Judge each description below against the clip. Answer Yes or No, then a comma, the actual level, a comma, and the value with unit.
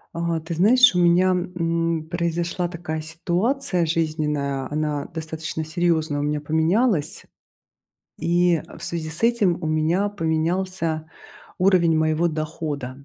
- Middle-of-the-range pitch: Yes, medium, 165 Hz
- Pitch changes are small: Yes, narrow, 2.1 semitones